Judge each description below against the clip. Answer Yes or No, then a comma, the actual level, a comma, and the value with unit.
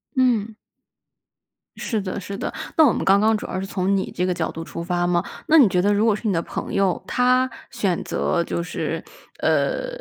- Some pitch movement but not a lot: Yes, average, 4.3 semitones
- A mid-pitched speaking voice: No, high, 200 Hz